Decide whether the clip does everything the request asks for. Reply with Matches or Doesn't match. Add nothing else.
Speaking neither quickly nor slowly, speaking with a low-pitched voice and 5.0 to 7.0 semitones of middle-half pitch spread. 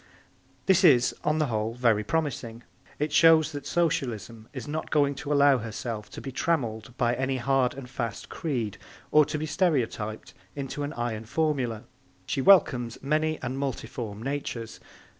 Doesn't match